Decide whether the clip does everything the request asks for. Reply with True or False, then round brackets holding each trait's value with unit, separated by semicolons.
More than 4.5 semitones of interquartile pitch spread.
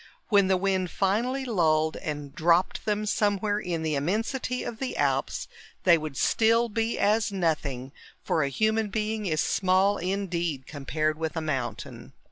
True (5.3 semitones)